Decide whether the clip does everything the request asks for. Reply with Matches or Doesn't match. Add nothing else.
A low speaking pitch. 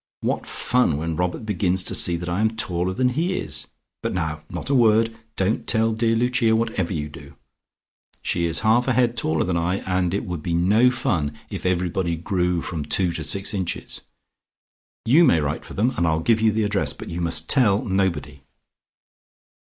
Matches